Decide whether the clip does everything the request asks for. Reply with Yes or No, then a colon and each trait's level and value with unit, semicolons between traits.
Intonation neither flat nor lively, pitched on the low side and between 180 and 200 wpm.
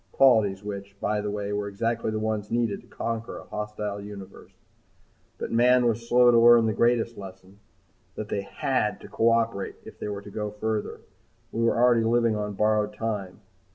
No: narrow, 2.1 semitones; low, 105 Hz; average, 185 wpm